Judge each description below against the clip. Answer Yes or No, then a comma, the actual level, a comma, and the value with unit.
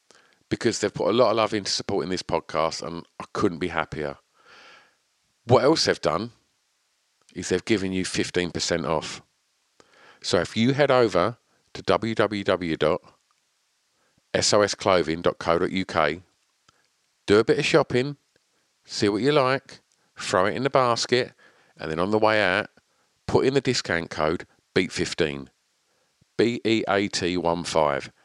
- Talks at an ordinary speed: No, slow, 125 wpm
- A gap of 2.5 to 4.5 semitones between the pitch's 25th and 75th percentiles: No, average, 5.0 semitones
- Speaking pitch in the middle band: No, very low, 95 Hz